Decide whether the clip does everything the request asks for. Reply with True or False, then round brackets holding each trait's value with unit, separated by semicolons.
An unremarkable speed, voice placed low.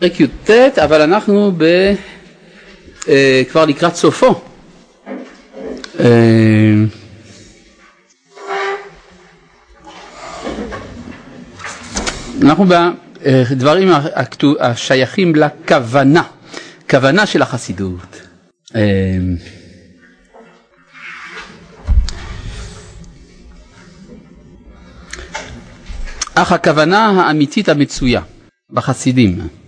False (40 wpm; 130 Hz)